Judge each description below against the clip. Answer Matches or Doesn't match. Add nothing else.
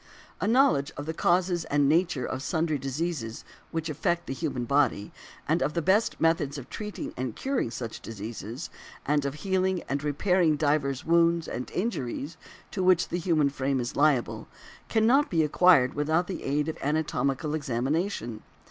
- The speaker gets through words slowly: Doesn't match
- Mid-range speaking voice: Matches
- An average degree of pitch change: Matches